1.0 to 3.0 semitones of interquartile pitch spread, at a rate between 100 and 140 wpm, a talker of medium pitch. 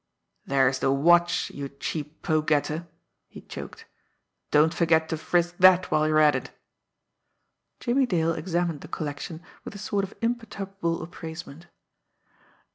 Yes: average, 2.7 semitones; slow, 135 wpm; medium, 165 Hz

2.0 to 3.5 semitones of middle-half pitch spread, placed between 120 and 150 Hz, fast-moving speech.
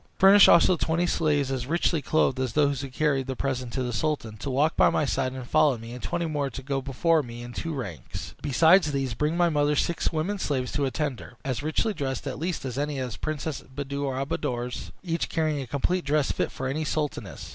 Yes: average, 3.2 semitones; medium, 140 Hz; fast, 230 wpm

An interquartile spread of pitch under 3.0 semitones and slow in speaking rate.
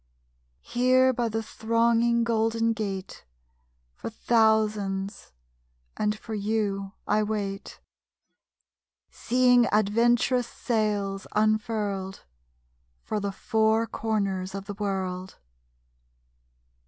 Yes: narrow, 2.5 semitones; slow, 85 wpm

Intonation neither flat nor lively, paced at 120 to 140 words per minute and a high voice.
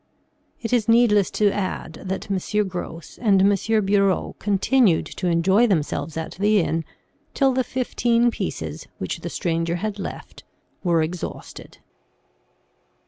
Yes: average, 4.1 semitones; slow, 135 wpm; high, 200 Hz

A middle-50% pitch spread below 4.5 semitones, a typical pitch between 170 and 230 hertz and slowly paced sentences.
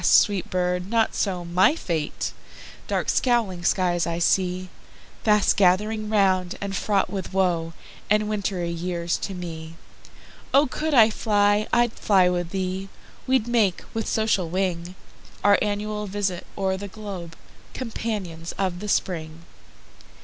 Yes: average, 3.0 semitones; high, 190 Hz; slow, 115 wpm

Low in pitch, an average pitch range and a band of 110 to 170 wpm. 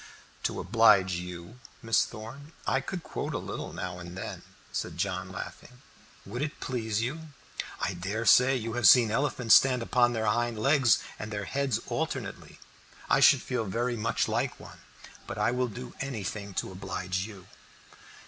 Yes: low, 115 Hz; average, 4.7 semitones; average, 165 wpm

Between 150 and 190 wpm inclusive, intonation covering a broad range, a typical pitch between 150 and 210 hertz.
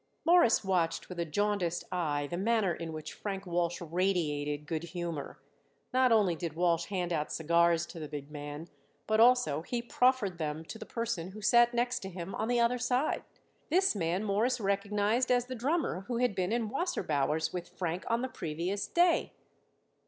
Yes: average, 180 wpm; wide, 5.9 semitones; high, 190 Hz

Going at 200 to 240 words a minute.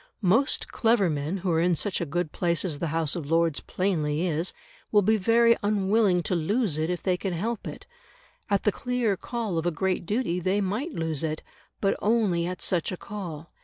Yes: fast, 205 wpm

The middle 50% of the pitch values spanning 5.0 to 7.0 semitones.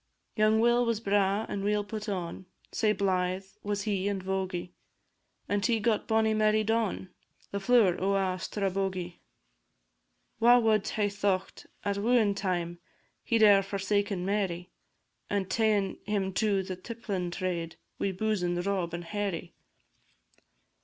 No: narrow, 2.4 semitones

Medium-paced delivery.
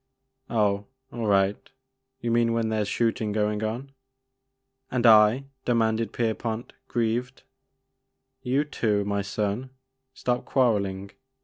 No: slow, 130 wpm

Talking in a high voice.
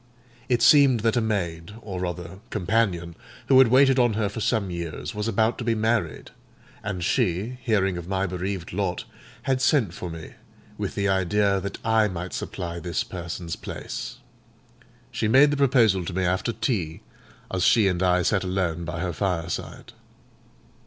No: very low, 95 Hz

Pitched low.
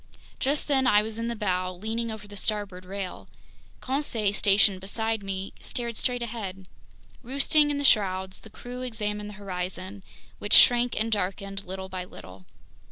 No: high, 210 Hz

